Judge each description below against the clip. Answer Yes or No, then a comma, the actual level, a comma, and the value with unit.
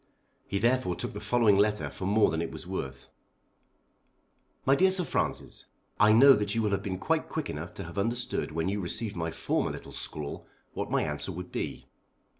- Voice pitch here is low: Yes, low, 100 Hz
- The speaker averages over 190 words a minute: Yes, average, 200 wpm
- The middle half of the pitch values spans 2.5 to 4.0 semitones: No, average, 4.5 semitones